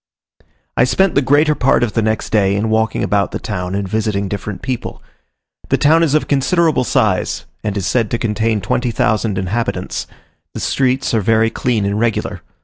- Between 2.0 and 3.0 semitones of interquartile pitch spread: No, average, 3.8 semitones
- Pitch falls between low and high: No, low, 110 Hz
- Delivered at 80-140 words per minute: No, average, 180 wpm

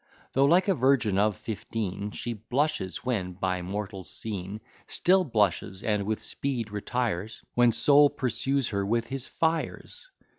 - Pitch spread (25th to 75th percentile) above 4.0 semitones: Yes, average, 5.1 semitones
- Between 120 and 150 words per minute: Yes, average, 145 wpm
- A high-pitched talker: No, low, 110 Hz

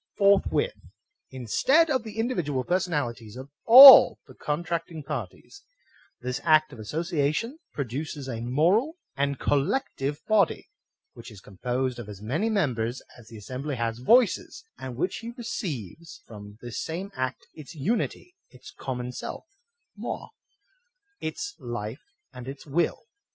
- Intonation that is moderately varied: No, wide, 7.7 semitones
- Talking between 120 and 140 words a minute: Yes, slow, 135 wpm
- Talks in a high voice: No, medium, 145 Hz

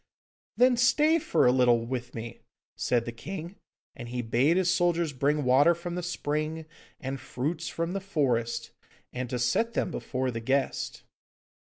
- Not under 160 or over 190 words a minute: Yes, average, 165 wpm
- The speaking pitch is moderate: Yes, medium, 145 Hz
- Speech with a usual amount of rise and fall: No, wide, 6.0 semitones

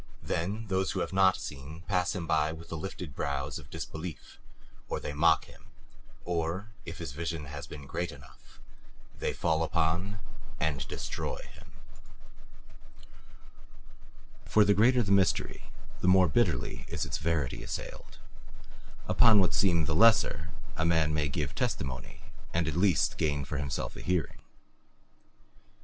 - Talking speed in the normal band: Yes, average, 145 wpm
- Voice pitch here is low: Yes, very low, 80 Hz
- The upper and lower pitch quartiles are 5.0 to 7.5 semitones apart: No, average, 3.7 semitones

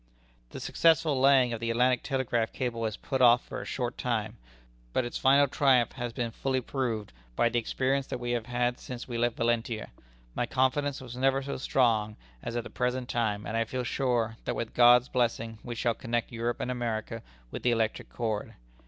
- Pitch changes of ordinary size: No, narrow, 1.9 semitones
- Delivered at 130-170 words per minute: No, fast, 205 wpm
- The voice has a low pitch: Yes, low, 120 Hz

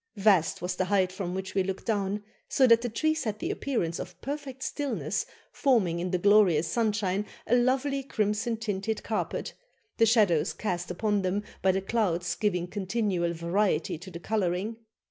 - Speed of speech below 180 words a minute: Yes, average, 170 wpm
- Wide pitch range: No, average, 3.8 semitones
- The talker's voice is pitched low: No, high, 205 Hz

